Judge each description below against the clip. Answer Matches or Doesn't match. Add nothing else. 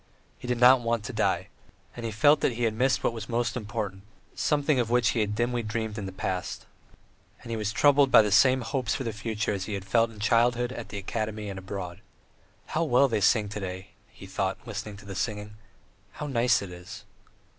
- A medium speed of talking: Doesn't match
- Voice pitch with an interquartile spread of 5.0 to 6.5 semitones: Doesn't match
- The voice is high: Doesn't match